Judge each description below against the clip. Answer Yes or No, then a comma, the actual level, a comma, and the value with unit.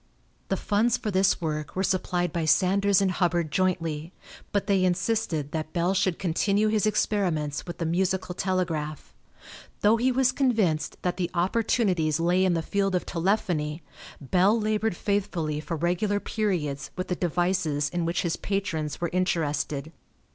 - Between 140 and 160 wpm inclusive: Yes, average, 155 wpm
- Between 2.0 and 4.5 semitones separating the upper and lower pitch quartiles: Yes, average, 3.7 semitones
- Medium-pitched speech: Yes, medium, 180 Hz